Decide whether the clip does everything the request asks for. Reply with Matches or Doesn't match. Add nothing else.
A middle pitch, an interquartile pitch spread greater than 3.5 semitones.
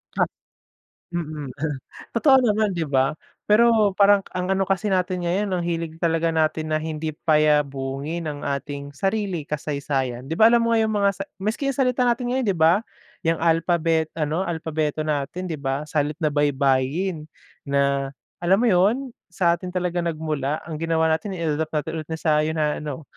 Matches